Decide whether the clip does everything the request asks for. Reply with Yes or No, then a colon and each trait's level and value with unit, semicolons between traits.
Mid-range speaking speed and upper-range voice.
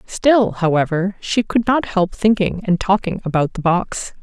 Yes: average, 170 wpm; high, 195 Hz